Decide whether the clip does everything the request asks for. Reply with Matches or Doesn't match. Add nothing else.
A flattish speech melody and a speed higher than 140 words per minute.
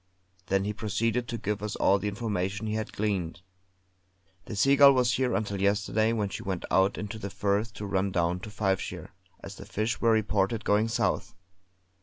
Matches